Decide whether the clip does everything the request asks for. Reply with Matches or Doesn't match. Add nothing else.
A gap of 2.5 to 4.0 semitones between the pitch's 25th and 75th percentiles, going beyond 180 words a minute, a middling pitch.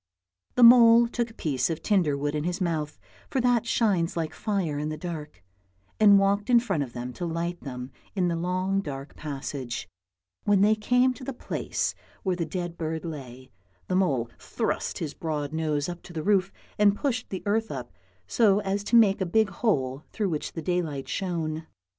Doesn't match